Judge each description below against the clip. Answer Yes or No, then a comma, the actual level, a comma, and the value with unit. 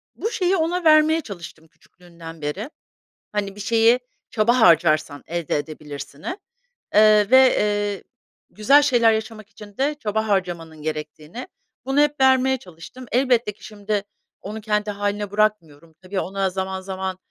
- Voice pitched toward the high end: Yes, high, 205 Hz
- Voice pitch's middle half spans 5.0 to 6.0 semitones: Yes, wide, 5.6 semitones